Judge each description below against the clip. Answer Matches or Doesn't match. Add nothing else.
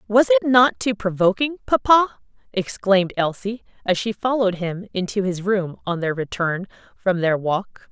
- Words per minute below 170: Matches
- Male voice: Doesn't match